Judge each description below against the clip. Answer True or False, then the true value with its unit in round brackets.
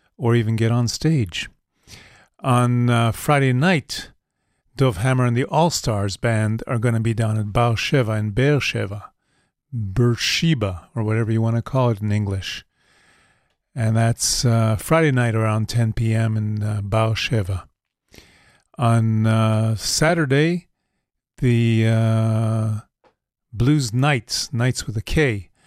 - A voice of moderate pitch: False (115 Hz)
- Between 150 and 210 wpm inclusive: False (135 wpm)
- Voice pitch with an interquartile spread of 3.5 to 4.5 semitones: False (2.5 semitones)